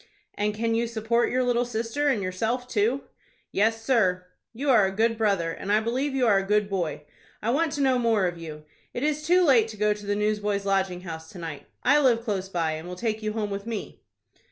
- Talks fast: Yes, fast, 230 wpm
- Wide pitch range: No, average, 3.6 semitones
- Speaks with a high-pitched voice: Yes, high, 215 Hz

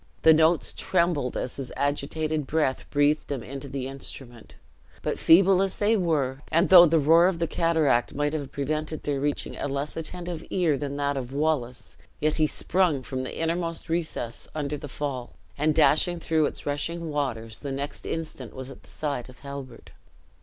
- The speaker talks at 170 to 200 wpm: Yes, average, 180 wpm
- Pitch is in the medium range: Yes, medium, 145 Hz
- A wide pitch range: No, average, 3.0 semitones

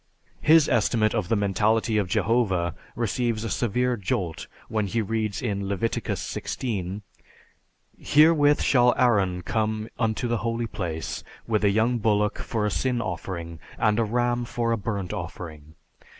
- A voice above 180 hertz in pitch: No, low, 110 Hz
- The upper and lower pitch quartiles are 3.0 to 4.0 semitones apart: Yes, average, 3.3 semitones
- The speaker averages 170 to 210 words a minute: No, average, 150 wpm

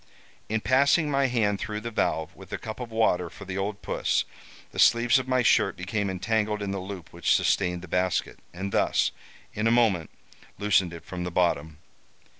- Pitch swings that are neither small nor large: Yes, average, 4.0 semitones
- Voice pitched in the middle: No, low, 105 Hz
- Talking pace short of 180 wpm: No, average, 195 wpm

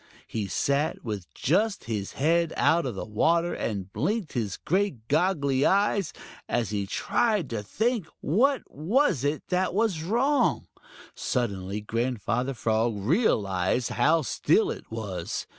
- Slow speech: Yes, slow, 130 wpm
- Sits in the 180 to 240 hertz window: No, medium, 140 Hz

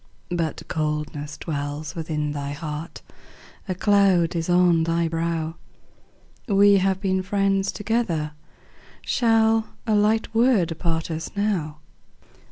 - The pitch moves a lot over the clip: No, average, 4.2 semitones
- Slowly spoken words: Yes, slow, 115 wpm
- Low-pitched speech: No, medium, 170 Hz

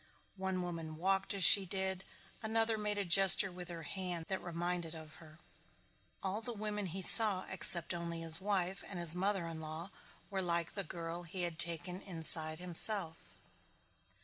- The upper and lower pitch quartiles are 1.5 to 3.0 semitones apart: Yes, narrow, 2.6 semitones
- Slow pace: No, average, 170 wpm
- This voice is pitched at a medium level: Yes, medium, 180 Hz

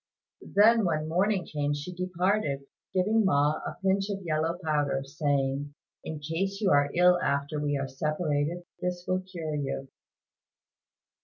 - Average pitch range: Yes, average, 4.1 semitones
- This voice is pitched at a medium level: Yes, medium, 160 Hz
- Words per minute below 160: Yes, average, 145 wpm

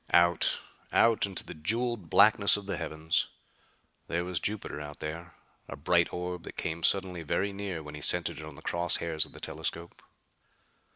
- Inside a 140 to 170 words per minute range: No, average, 180 wpm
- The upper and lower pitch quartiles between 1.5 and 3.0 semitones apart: No, average, 3.6 semitones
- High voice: No, very low, 85 Hz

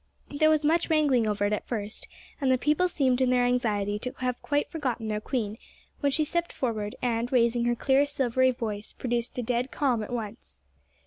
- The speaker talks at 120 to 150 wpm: No, average, 200 wpm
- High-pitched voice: Yes, high, 245 Hz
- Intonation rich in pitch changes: No, average, 3.8 semitones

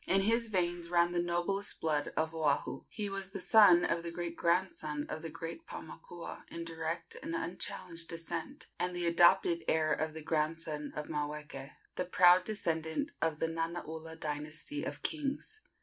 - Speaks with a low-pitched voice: No, medium, 170 Hz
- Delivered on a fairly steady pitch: Yes, narrow, 2.2 semitones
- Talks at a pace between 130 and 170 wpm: Yes, average, 165 wpm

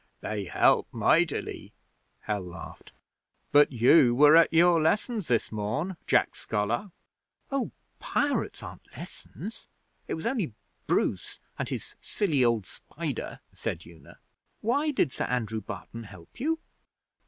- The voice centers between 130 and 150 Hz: Yes, medium, 140 Hz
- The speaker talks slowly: Yes, slow, 130 wpm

